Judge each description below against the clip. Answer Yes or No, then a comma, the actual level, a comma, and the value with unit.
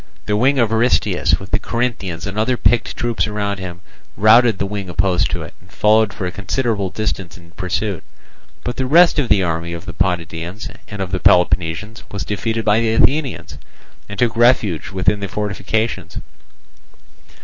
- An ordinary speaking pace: Yes, average, 175 wpm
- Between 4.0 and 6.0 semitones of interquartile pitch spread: No, average, 3.6 semitones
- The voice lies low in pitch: Yes, low, 105 Hz